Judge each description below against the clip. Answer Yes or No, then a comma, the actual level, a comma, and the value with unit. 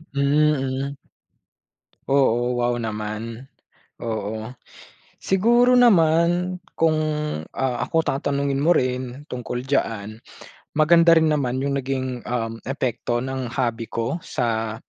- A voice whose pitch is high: No, low, 130 Hz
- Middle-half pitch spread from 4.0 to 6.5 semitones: Yes, average, 4.3 semitones